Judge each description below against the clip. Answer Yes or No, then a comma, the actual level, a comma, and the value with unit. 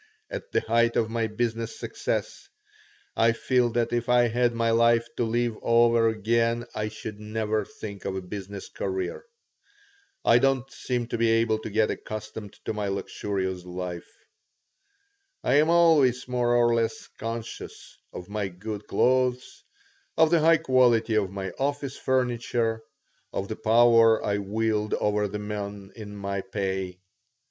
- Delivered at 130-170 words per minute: Yes, average, 155 wpm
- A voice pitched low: Yes, low, 115 Hz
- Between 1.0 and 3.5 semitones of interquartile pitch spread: Yes, narrow, 2.6 semitones